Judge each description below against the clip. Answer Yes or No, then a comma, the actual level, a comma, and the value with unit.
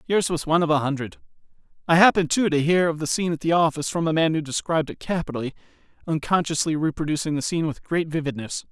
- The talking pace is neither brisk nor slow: No, fast, 215 wpm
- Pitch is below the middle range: No, medium, 160 Hz